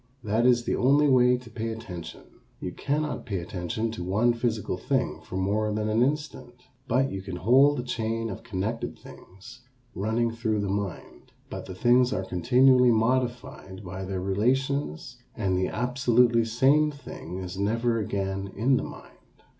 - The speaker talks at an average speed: Yes, average, 165 wpm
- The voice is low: Yes, low, 115 Hz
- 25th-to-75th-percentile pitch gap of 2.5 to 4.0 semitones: No, average, 4.4 semitones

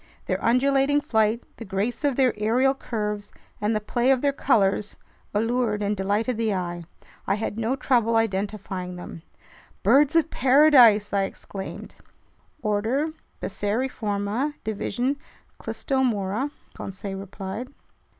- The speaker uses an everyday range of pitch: Yes, average, 4.2 semitones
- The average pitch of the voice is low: No, high, 220 Hz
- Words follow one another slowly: Yes, slow, 120 wpm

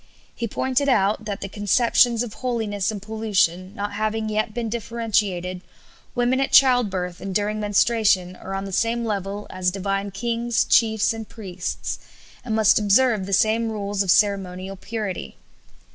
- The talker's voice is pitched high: Yes, high, 210 Hz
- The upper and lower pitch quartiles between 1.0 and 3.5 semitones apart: Yes, average, 2.8 semitones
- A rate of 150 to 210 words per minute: Yes, average, 155 wpm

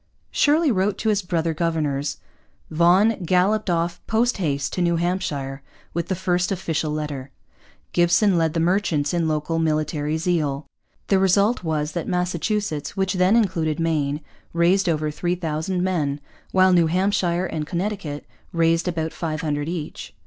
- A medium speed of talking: Yes, average, 145 wpm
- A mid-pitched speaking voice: Yes, medium, 170 Hz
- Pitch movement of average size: Yes, average, 3.3 semitones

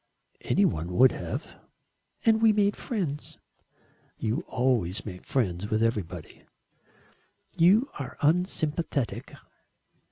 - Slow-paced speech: Yes, slow, 100 wpm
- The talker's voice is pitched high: No, low, 130 Hz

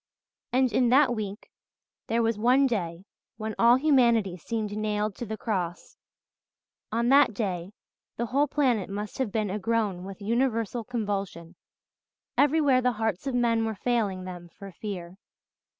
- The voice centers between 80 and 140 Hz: No, high, 220 Hz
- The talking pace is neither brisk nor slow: Yes, average, 150 wpm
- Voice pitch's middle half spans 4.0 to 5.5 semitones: No, average, 3.6 semitones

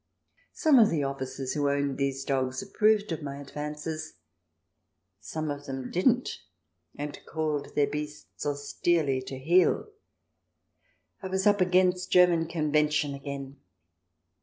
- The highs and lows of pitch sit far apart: No, average, 4.3 semitones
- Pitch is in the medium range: Yes, medium, 150 Hz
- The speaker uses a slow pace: Yes, slow, 125 wpm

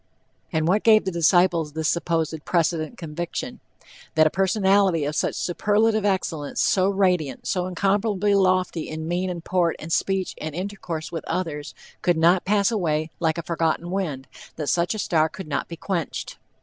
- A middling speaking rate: Yes, average, 170 wpm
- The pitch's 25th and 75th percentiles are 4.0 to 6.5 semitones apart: No, average, 3.2 semitones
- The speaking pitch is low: No, medium, 175 Hz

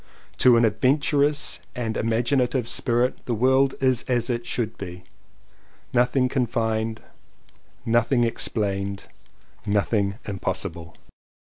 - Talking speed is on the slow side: Yes, slow, 110 wpm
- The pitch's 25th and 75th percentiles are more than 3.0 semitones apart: No, narrow, 2.6 semitones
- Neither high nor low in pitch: No, low, 120 Hz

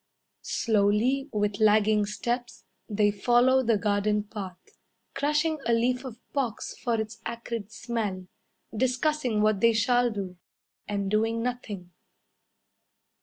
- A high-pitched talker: Yes, high, 225 Hz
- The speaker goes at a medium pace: No, slow, 120 wpm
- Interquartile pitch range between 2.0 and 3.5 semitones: Yes, average, 2.8 semitones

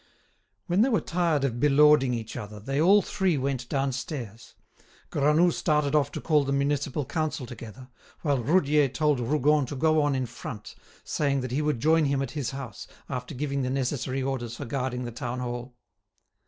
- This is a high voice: No, medium, 140 Hz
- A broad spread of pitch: No, average, 3.2 semitones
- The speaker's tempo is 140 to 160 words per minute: No, average, 180 wpm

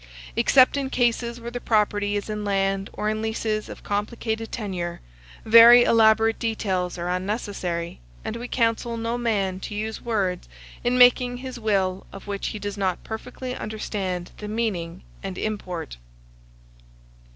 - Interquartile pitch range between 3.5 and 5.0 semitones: No, average, 3.1 semitones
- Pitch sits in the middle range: No, high, 215 Hz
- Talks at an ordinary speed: Yes, average, 150 wpm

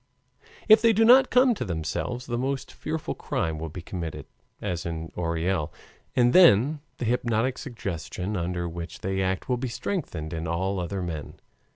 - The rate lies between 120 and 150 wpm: No, average, 170 wpm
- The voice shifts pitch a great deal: Yes, wide, 7.4 semitones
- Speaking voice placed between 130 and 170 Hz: No, very low, 95 Hz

